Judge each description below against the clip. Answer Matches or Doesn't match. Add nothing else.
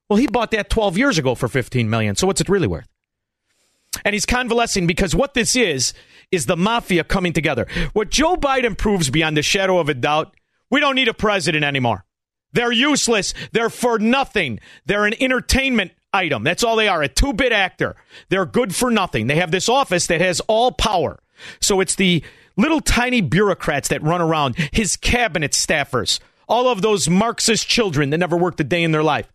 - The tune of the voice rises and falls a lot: Matches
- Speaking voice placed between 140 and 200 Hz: Matches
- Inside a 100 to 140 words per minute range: Doesn't match